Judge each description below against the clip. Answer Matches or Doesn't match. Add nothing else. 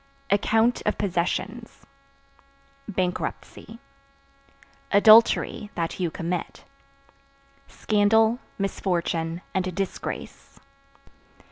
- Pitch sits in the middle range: Doesn't match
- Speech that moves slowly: Matches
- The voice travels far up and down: Doesn't match